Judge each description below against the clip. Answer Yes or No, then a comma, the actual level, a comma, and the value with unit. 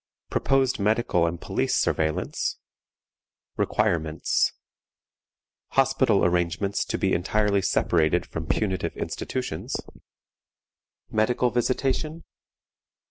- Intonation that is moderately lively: No, wide, 6.4 semitones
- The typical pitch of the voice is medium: No, low, 100 Hz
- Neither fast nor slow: No, slow, 80 wpm